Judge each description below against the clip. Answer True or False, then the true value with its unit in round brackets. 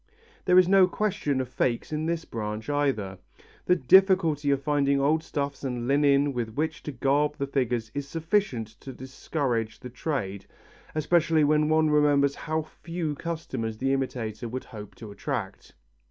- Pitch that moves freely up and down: False (4.1 semitones)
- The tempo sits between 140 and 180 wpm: True (160 wpm)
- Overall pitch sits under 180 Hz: True (140 Hz)